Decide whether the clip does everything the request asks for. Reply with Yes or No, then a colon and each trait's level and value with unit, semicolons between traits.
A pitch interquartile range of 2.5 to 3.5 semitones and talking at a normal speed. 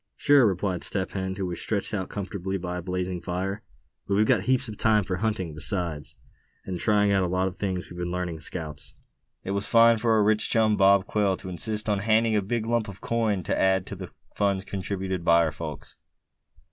No: average, 2.9 semitones; fast, 220 wpm